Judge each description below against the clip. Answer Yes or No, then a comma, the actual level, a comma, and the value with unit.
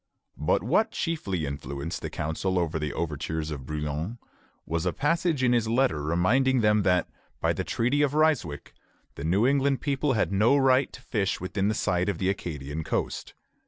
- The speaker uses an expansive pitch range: Yes, wide, 8.6 semitones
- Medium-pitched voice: No, very low, 95 Hz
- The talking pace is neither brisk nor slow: Yes, average, 175 wpm